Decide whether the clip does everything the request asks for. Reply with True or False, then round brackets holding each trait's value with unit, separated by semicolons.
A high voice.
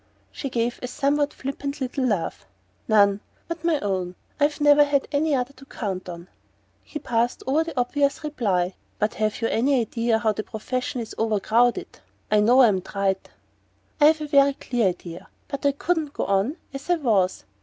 True (245 Hz)